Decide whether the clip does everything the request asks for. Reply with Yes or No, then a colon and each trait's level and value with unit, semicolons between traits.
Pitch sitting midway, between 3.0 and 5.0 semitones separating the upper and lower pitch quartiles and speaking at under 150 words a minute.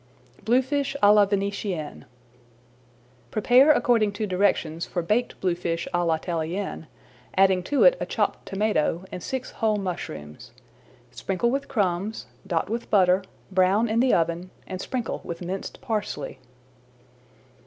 No: high, 195 Hz; average, 4.3 semitones; slow, 135 wpm